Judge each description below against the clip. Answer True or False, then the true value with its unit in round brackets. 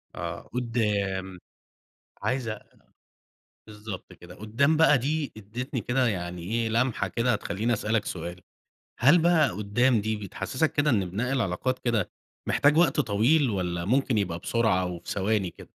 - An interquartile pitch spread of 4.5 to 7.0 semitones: True (5.1 semitones)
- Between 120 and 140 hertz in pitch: False (110 Hz)